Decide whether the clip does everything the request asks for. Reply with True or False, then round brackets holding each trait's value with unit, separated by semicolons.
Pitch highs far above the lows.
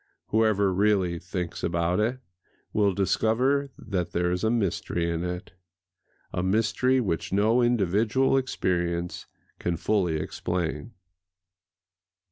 False (4.0 semitones)